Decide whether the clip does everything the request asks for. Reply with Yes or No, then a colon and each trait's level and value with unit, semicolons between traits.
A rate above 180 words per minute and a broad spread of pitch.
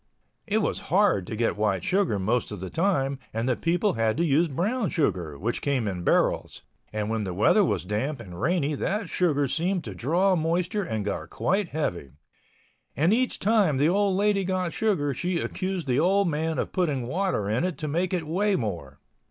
Yes: average, 200 wpm; wide, 8.7 semitones